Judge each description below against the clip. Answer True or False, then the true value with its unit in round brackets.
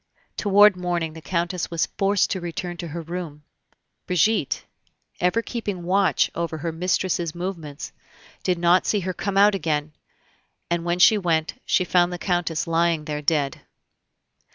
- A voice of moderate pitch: True (175 Hz)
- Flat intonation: True (2.3 semitones)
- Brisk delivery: False (155 wpm)